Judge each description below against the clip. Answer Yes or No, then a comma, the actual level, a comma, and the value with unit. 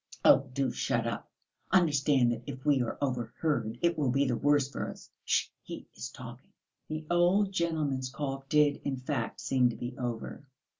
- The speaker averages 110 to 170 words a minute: No, average, 180 wpm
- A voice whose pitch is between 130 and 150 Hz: Yes, low, 135 Hz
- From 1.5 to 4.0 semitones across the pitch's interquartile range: Yes, average, 3.1 semitones